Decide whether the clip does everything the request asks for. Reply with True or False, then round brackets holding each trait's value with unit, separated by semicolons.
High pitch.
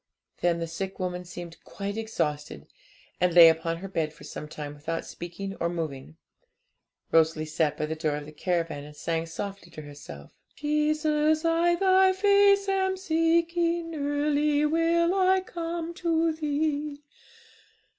True (225 Hz)